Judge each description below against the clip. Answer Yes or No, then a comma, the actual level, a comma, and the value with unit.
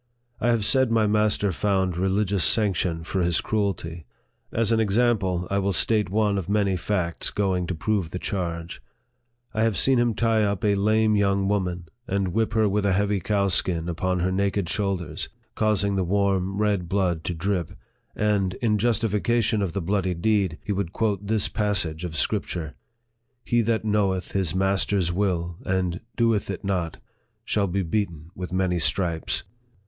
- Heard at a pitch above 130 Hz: No, low, 100 Hz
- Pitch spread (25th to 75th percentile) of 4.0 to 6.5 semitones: No, average, 2.8 semitones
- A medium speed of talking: Yes, average, 170 wpm